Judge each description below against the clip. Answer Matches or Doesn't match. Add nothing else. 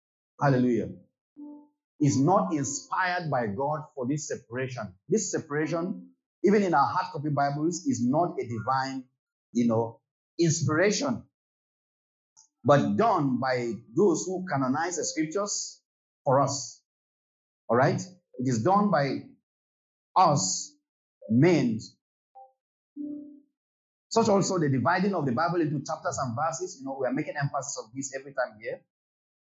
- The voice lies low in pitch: Doesn't match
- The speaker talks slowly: Matches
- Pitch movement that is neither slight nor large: Doesn't match